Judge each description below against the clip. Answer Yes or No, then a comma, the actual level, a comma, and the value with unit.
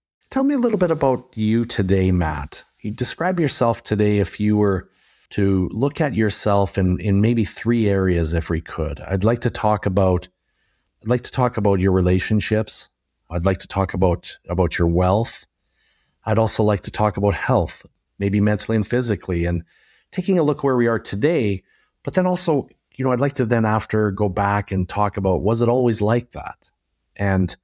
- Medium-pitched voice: No, low, 105 Hz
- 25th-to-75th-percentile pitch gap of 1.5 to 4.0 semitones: Yes, average, 3.7 semitones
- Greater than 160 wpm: Yes, average, 190 wpm